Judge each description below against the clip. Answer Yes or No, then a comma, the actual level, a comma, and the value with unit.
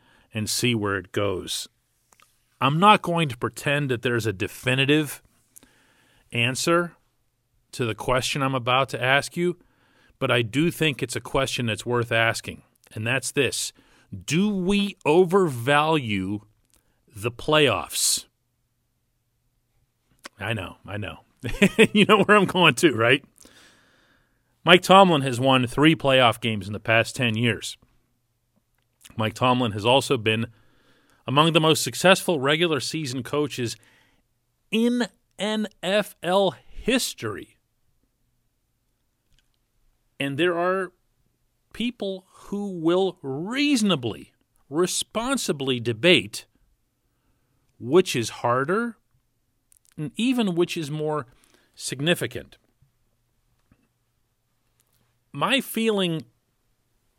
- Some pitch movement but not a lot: No, wide, 6.3 semitones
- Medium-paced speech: No, slow, 105 wpm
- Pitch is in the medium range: No, low, 130 Hz